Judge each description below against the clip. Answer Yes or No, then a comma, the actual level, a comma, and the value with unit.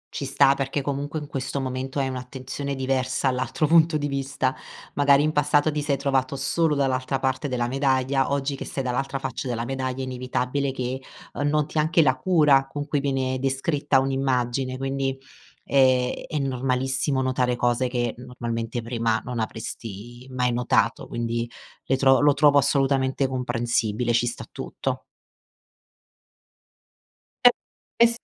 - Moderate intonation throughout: No, narrow, 1.8 semitones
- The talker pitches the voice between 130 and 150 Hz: Yes, low, 135 Hz